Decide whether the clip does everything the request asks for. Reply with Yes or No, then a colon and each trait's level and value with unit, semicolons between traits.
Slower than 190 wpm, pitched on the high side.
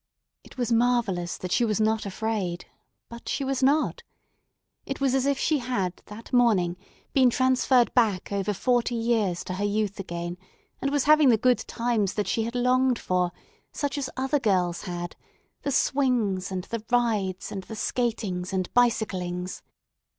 Yes: average, 165 wpm; high, 225 Hz